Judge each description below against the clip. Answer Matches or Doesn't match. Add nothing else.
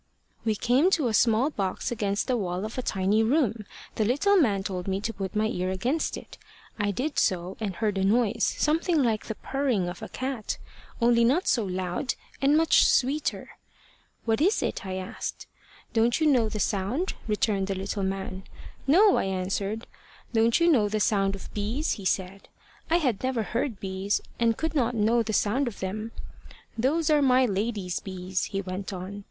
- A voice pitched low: Doesn't match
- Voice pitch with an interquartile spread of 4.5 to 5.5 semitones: Matches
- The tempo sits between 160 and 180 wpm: Doesn't match